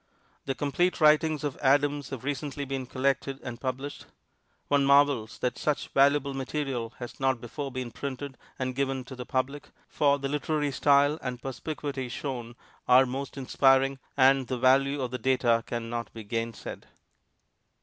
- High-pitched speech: No, low, 135 Hz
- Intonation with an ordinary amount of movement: No, narrow, 2.0 semitones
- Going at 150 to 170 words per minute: Yes, average, 160 wpm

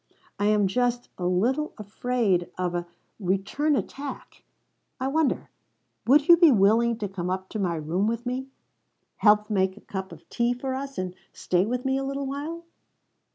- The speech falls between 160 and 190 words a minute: Yes, average, 180 wpm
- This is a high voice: Yes, high, 230 Hz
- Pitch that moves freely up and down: Yes, wide, 5.8 semitones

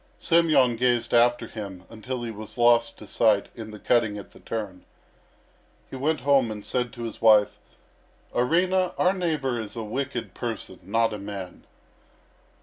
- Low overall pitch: Yes, low, 115 Hz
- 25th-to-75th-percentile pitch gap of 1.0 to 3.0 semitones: No, average, 3.4 semitones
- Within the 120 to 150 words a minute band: No, average, 160 wpm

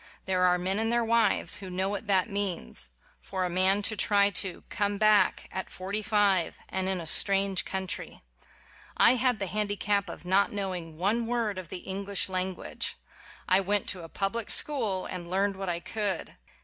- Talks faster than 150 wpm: Yes, average, 185 wpm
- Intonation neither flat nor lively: No, narrow, 1.9 semitones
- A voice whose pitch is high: Yes, high, 195 Hz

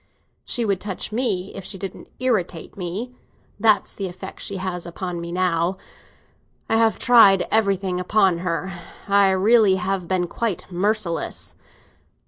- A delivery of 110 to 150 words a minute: Yes, average, 140 wpm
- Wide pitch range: No, average, 2.9 semitones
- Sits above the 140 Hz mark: Yes, high, 190 Hz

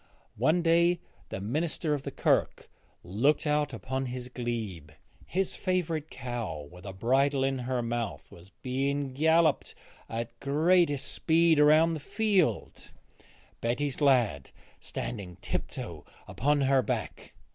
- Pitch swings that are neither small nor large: Yes, average, 4.8 semitones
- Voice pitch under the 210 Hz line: Yes, low, 135 Hz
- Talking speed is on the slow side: Yes, slow, 130 wpm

